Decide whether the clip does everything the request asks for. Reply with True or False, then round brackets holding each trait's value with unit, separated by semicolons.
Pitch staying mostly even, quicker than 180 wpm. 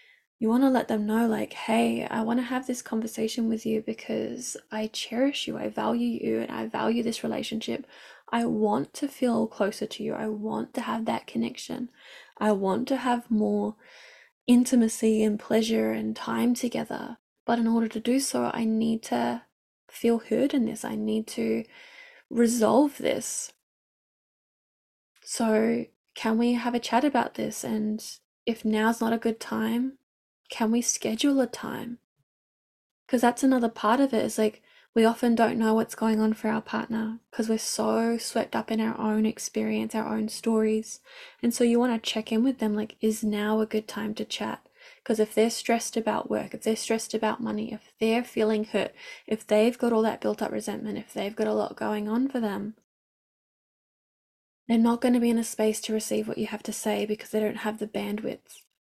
True (1.6 semitones; 195 wpm)